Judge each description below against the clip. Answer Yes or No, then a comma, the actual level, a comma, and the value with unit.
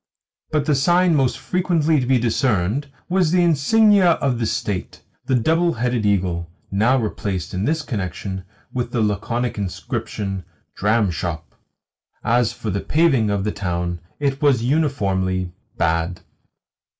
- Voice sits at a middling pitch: No, low, 115 Hz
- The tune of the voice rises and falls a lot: Yes, wide, 7.0 semitones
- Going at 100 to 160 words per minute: Yes, average, 140 wpm